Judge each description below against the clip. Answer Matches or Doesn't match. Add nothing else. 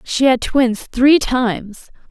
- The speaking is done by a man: Doesn't match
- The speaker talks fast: Doesn't match